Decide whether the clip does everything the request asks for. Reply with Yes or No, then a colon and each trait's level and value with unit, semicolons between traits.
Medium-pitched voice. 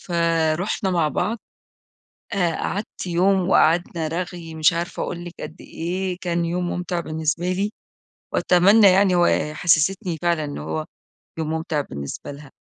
Yes: medium, 170 Hz